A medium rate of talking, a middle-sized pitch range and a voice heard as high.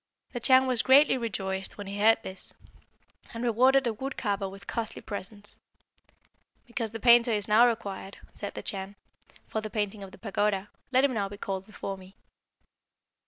Yes: average, 175 wpm; average, 3.2 semitones; high, 215 Hz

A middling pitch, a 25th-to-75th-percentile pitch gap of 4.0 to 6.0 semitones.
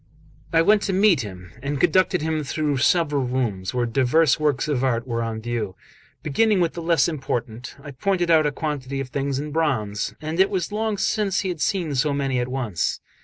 Yes: medium, 145 Hz; average, 5.0 semitones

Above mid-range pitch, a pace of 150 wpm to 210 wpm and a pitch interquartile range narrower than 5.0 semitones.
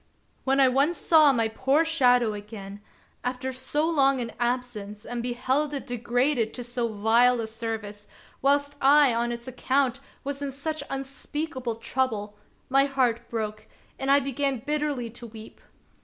Yes: very high, 250 Hz; average, 155 wpm; average, 3.1 semitones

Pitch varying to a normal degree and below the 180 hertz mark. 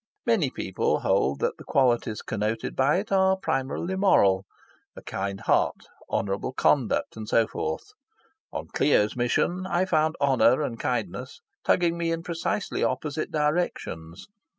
No: wide, 7.9 semitones; medium, 140 Hz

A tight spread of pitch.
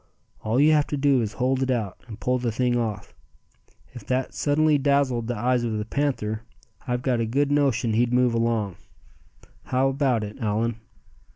No: average, 3.1 semitones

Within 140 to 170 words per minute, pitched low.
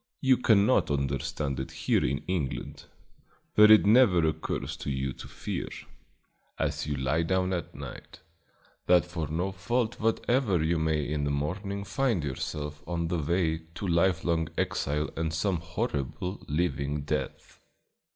Yes: average, 145 wpm; very low, 85 Hz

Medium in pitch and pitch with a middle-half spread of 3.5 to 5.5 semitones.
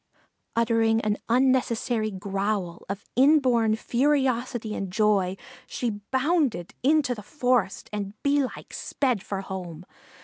No: high, 225 Hz; average, 4.4 semitones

